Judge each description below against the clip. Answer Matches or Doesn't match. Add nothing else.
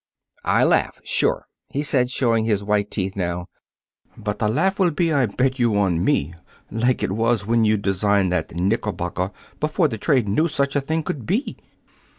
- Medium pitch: Doesn't match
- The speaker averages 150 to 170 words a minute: Doesn't match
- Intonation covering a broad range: Matches